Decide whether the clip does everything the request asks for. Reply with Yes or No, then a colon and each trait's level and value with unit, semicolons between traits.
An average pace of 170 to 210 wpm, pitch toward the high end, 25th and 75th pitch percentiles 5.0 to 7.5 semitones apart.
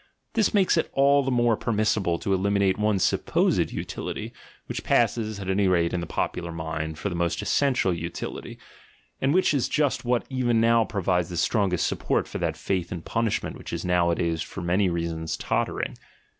No: average, 185 wpm; very low, 95 Hz; wide, 5.4 semitones